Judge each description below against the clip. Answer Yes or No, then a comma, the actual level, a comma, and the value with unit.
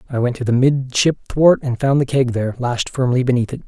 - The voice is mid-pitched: No, low, 130 Hz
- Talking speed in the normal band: No, fast, 245 wpm